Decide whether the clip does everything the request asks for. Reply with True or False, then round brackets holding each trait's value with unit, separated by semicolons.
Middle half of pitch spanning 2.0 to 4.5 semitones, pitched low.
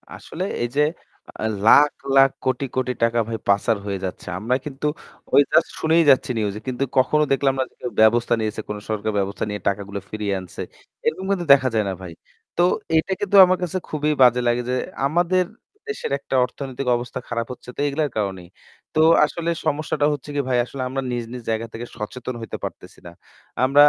False (5.0 semitones; 125 Hz)